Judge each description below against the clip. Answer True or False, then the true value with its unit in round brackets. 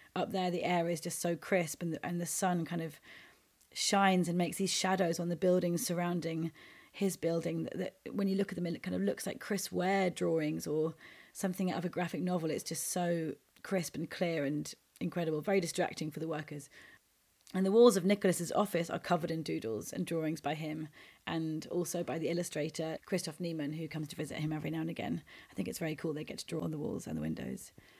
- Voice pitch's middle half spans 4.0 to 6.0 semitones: False (2.4 semitones)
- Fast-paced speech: True (225 wpm)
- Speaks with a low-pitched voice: False (170 Hz)